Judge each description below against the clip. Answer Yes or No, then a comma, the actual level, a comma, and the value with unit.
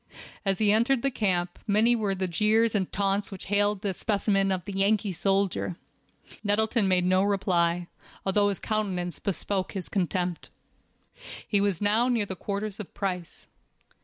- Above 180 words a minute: No, average, 160 wpm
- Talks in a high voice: Yes, high, 200 Hz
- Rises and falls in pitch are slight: Yes, narrow, 2.2 semitones